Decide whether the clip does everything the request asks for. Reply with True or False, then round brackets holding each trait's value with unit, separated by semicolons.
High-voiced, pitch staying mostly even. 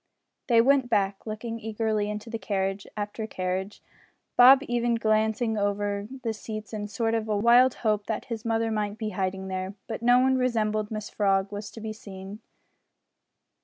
True (215 Hz; 2.0 semitones)